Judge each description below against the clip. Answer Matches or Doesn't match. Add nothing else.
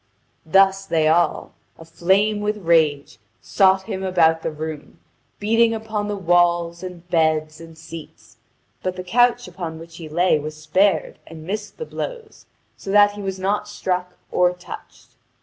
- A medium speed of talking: Matches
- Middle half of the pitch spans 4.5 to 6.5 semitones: Doesn't match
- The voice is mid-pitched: Matches